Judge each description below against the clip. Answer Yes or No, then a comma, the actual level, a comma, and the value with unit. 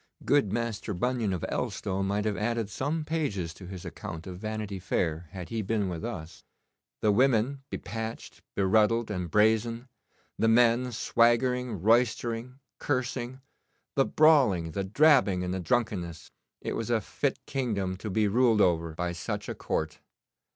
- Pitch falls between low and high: No, low, 110 Hz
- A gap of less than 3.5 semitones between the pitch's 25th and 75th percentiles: No, average, 4.6 semitones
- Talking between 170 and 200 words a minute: No, average, 160 wpm